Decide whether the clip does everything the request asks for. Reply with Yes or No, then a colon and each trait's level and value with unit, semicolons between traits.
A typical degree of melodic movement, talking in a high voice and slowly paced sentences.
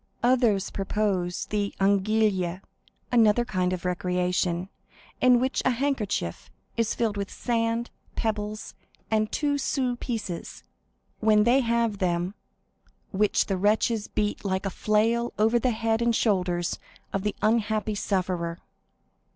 Yes: average, 3.6 semitones; high, 210 Hz; slow, 125 wpm